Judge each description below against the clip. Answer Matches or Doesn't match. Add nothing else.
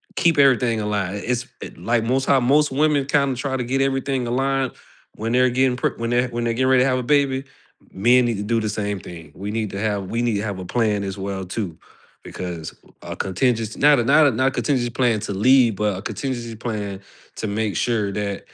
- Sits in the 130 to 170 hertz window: Doesn't match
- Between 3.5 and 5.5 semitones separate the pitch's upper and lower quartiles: Matches